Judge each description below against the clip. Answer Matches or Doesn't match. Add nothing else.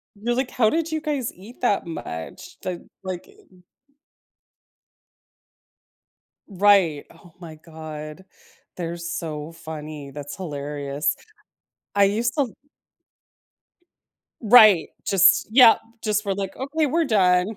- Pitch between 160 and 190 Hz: Matches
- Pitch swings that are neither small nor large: Doesn't match